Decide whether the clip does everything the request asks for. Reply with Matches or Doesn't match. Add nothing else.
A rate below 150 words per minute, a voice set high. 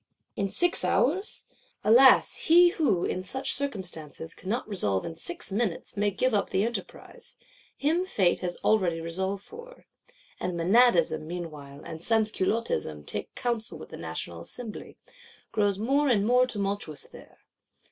Matches